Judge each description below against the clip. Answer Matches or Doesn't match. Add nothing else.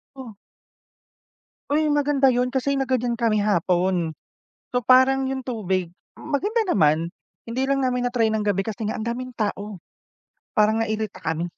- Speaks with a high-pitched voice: Matches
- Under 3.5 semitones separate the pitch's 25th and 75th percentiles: Doesn't match